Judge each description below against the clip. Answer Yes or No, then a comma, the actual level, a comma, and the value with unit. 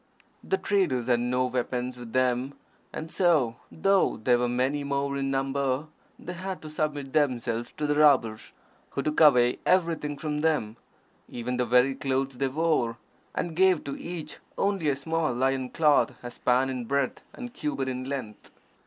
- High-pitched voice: No, low, 135 Hz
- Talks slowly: No, average, 170 wpm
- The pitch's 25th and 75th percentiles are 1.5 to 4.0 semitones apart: Yes, average, 3.5 semitones